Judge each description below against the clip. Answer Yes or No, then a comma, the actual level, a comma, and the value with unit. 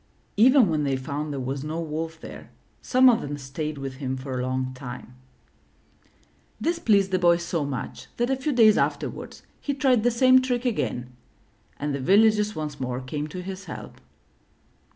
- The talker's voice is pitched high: No, medium, 160 Hz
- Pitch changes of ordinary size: No, wide, 8.5 semitones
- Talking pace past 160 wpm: Yes, average, 180 wpm